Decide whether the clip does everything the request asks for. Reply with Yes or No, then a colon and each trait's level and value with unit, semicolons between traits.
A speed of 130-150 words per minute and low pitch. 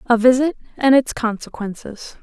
No: slow, 135 wpm; high, 240 Hz